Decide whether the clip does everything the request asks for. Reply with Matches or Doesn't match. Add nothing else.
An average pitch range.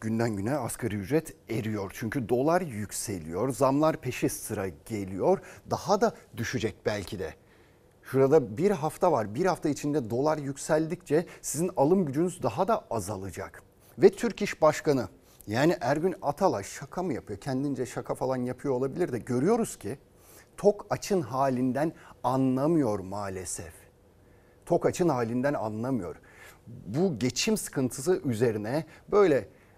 Doesn't match